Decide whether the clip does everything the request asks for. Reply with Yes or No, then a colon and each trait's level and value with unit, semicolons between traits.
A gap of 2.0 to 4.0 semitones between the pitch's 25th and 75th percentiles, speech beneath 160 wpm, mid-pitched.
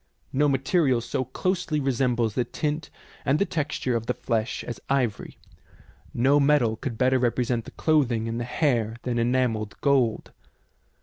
No: average, 3.3 semitones; average, 150 wpm; low, 125 Hz